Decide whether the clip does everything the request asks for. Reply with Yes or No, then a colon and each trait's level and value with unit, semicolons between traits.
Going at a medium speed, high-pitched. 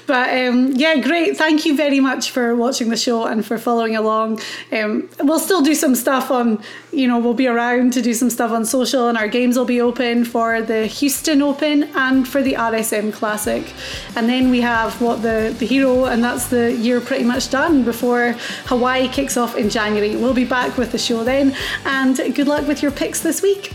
No: fast, 215 wpm; very high, 250 Hz